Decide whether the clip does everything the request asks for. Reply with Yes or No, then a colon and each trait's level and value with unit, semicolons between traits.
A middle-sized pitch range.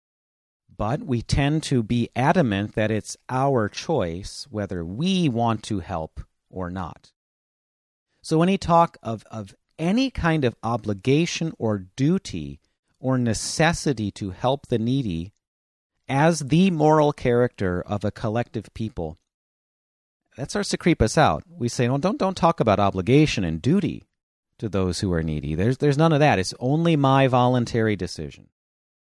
No: wide, 7.3 semitones